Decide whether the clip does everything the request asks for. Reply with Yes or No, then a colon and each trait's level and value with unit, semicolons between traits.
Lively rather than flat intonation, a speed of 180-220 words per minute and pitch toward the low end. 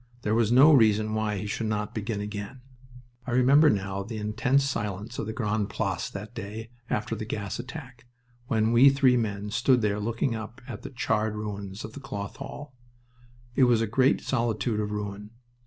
No: average, 2.9 semitones; average, 190 wpm; low, 110 Hz